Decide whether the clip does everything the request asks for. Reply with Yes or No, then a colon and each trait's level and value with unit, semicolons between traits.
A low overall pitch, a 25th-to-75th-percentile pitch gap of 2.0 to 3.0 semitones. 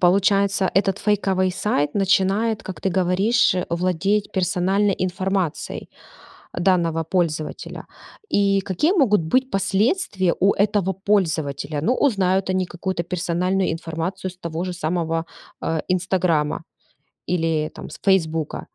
No: medium, 185 Hz; average, 2.7 semitones